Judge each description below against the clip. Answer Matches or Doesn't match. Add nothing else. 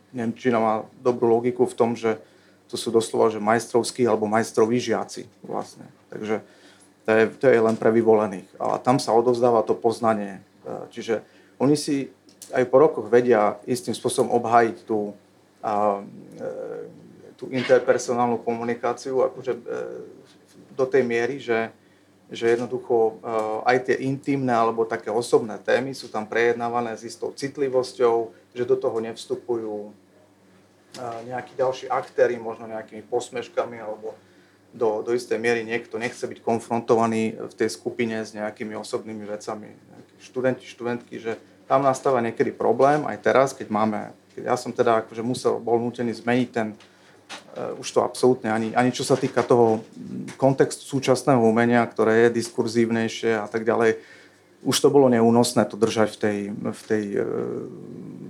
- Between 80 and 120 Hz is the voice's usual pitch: Matches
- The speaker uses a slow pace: Doesn't match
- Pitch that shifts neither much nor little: Doesn't match